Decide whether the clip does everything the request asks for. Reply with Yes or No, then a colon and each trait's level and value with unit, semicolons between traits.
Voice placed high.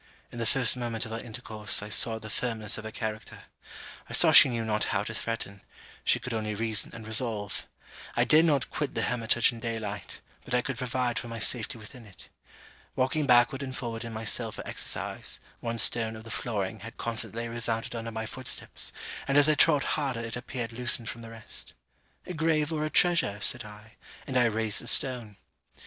No: low, 115 Hz